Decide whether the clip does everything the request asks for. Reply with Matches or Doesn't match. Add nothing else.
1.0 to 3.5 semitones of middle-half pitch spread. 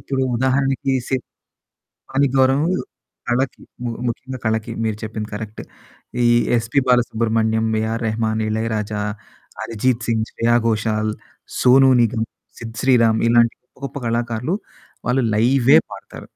Matches